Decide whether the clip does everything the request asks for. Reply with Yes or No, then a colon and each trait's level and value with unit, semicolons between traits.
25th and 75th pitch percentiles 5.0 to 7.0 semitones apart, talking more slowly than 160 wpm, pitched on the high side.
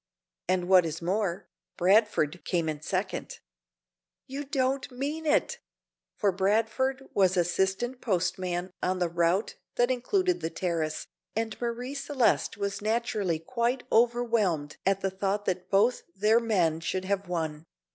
Yes: average, 5.3 semitones; slow, 135 wpm; high, 200 Hz